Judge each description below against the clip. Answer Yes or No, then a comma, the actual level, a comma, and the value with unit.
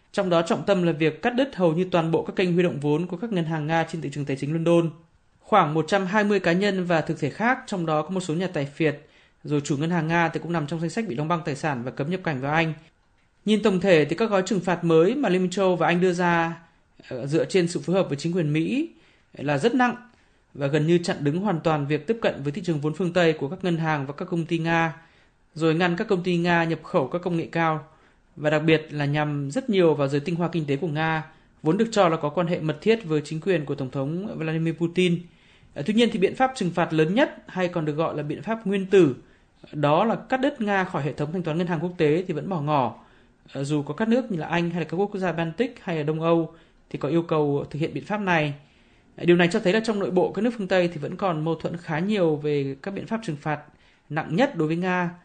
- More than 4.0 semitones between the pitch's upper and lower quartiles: No, average, 3.2 semitones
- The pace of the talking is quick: Yes, fast, 280 wpm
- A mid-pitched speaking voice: Yes, medium, 170 Hz